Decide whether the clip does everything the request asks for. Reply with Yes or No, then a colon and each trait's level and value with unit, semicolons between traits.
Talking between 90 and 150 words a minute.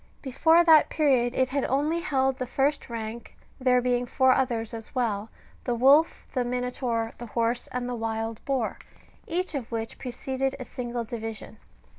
No: average, 165 wpm